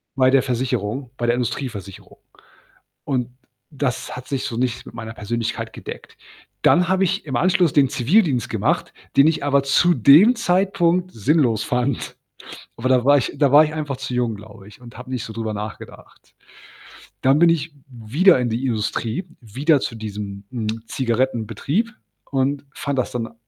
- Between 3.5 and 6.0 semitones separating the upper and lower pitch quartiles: Yes, average, 4.3 semitones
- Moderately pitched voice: No, low, 130 Hz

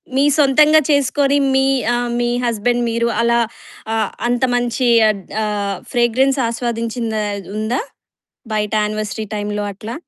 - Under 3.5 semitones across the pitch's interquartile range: Yes, average, 3.0 semitones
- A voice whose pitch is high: Yes, high, 235 Hz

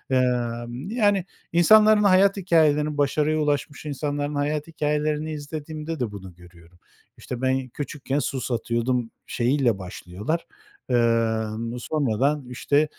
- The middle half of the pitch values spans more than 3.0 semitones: Yes, average, 4.5 semitones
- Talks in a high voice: No, medium, 145 Hz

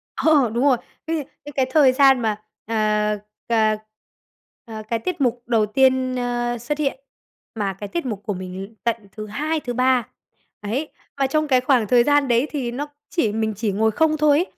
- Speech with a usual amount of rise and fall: Yes, average, 4.4 semitones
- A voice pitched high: Yes, high, 245 Hz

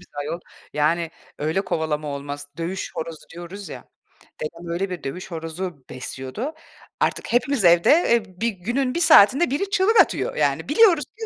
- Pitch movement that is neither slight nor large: No, wide, 7.8 semitones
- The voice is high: No, medium, 175 Hz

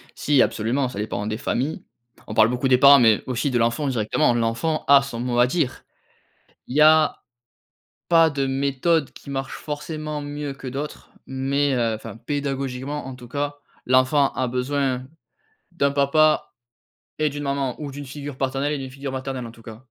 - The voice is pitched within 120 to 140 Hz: Yes, low, 135 Hz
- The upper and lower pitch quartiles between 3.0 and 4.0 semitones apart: No, narrow, 2.4 semitones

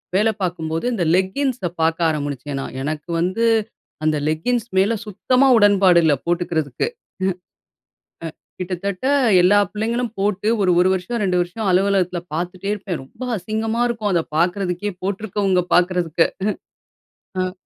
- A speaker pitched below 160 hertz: No, medium, 185 Hz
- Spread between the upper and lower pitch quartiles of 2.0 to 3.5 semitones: Yes, average, 3.2 semitones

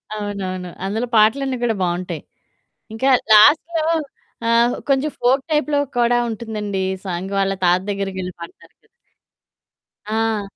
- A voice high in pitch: Yes, high, 215 Hz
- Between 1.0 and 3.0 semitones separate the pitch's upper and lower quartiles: No, average, 4.1 semitones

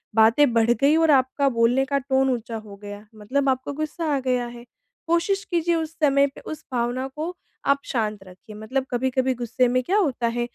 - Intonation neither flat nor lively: Yes, average, 3.5 semitones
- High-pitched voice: Yes, very high, 260 Hz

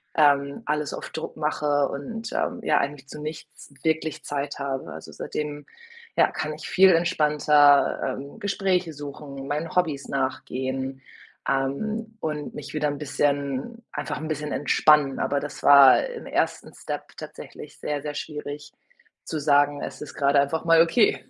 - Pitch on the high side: No, medium, 145 Hz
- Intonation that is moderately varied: No, narrow, 2.0 semitones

